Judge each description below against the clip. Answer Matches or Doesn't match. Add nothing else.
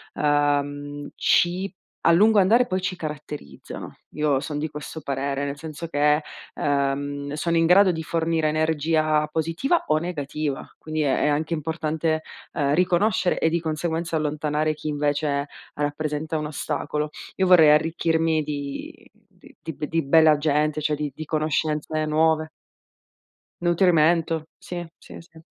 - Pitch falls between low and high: Matches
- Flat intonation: Matches